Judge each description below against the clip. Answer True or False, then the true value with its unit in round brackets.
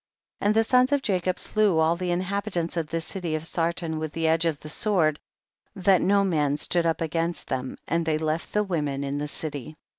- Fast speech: True (220 wpm)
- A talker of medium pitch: True (165 Hz)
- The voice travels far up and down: False (3.2 semitones)